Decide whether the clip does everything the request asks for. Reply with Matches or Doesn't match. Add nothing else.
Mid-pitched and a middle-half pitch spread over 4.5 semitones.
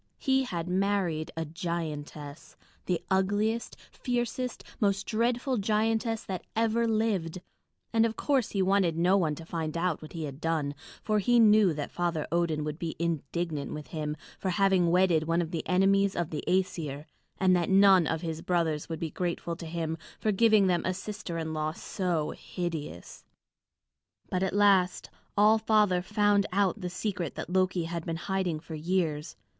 Doesn't match